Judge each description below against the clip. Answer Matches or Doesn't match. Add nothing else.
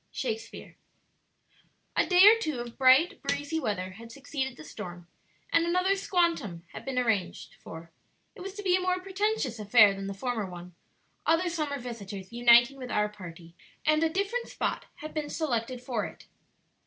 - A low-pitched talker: Doesn't match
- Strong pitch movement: Matches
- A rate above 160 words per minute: Matches